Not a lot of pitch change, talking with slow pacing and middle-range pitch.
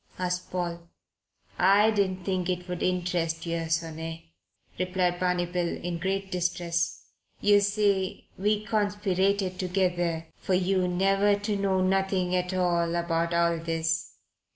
Yes: narrow, 2.1 semitones; slow, 130 wpm; medium, 180 Hz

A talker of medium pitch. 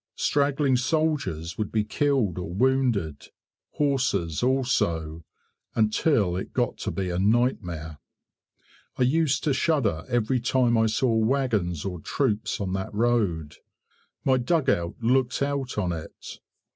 No: low, 115 Hz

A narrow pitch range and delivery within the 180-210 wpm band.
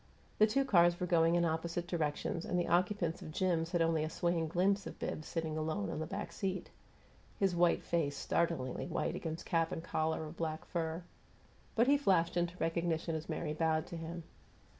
Yes: narrow, 1.6 semitones; average, 195 wpm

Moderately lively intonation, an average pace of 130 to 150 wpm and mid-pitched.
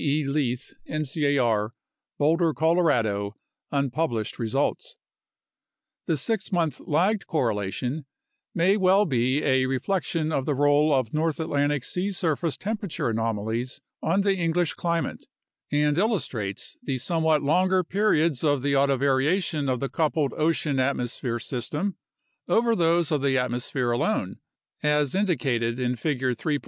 Yes: average, 4.6 semitones; slow, 135 wpm; medium, 145 Hz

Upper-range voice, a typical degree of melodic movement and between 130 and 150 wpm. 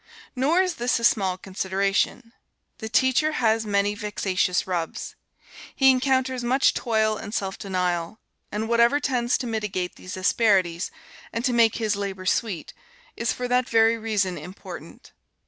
Yes: high, 220 Hz; average, 4.1 semitones; average, 145 wpm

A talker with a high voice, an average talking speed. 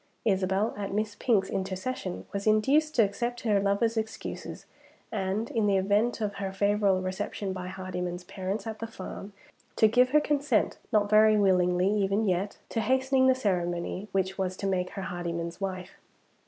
Yes: high, 200 Hz; average, 165 wpm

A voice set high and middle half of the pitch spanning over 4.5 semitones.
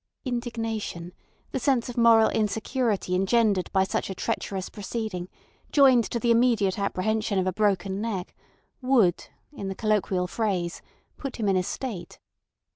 No: high, 215 Hz; average, 3.7 semitones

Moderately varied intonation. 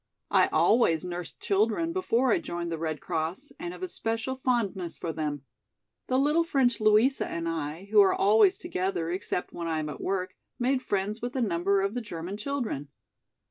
No: wide, 6.5 semitones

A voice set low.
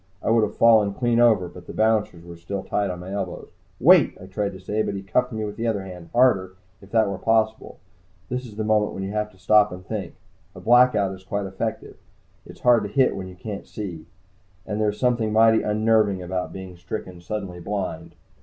Yes: low, 105 Hz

